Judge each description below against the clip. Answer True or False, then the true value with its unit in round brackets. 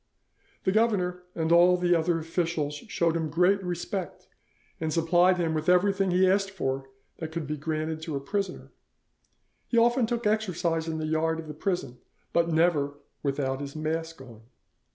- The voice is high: False (165 Hz)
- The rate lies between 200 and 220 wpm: False (170 wpm)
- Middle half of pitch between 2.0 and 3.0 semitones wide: True (2.7 semitones)